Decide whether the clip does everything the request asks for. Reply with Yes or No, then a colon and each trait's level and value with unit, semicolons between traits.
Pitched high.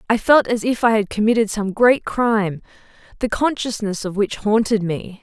Yes: high, 215 Hz